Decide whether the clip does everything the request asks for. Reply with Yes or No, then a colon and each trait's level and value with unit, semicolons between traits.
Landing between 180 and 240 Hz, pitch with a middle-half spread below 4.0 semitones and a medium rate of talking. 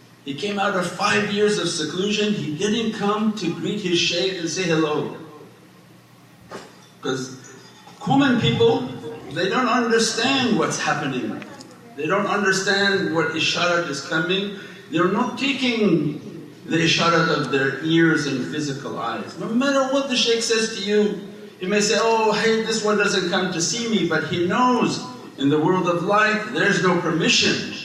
No: high, 190 Hz; average, 4.7 semitones; average, 160 wpm